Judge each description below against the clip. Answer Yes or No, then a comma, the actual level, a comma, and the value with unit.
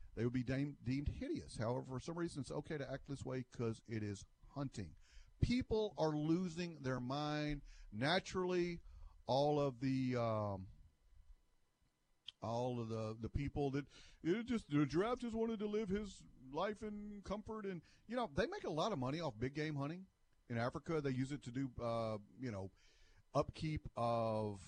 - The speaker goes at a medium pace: Yes, average, 180 wpm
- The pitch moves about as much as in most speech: No, wide, 6.7 semitones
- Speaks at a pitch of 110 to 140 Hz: Yes, low, 135 Hz